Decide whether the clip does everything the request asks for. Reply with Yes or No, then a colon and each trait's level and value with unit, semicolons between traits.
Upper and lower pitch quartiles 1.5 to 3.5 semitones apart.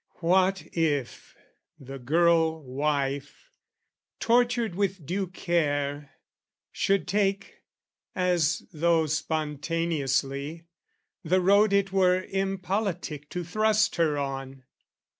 No: average, 4.8 semitones